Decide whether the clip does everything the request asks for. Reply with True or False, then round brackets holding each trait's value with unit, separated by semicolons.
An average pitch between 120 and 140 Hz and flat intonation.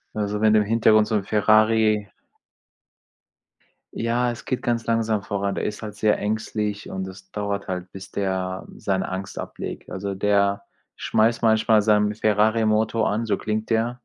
False (105 Hz; 1.7 semitones)